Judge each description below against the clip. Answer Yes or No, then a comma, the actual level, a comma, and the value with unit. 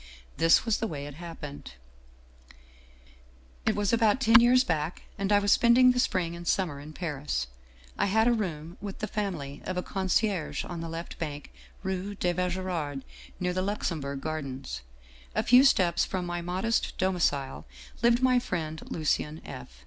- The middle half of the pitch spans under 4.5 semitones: No, wide, 5.5 semitones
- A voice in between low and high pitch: Yes, medium, 175 Hz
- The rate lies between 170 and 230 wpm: Yes, average, 175 wpm